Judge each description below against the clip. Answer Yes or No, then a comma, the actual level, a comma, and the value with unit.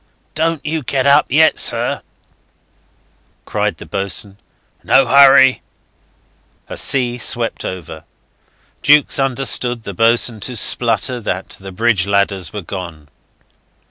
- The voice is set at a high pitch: No, low, 120 Hz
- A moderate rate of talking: No, slow, 115 wpm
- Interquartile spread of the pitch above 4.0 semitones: Yes, wide, 5.5 semitones